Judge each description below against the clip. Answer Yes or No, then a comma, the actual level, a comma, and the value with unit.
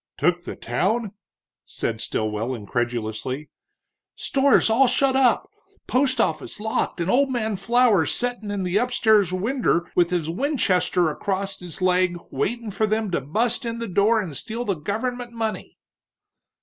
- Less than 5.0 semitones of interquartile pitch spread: No, wide, 5.6 semitones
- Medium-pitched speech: No, high, 205 Hz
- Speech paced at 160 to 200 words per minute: No, average, 150 wpm